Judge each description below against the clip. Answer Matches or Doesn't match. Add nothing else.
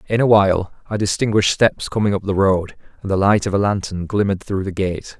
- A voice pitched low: Matches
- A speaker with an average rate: Doesn't match